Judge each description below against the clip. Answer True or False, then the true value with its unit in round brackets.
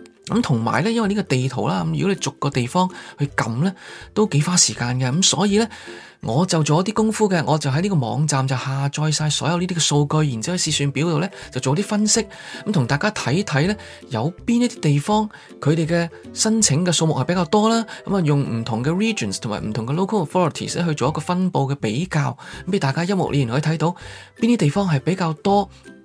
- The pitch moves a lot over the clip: True (5.8 semitones)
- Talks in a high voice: False (160 Hz)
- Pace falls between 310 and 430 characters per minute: True (380 characters per minute)